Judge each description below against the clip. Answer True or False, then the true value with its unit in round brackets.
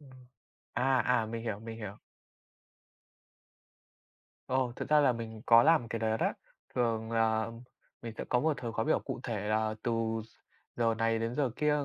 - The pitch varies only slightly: True (2.0 semitones)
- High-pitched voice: False (115 Hz)